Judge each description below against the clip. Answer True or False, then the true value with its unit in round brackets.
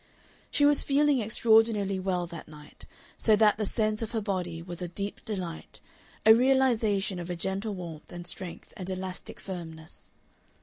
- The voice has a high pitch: True (195 Hz)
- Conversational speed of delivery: True (165 wpm)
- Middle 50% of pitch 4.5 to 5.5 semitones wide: False (3.9 semitones)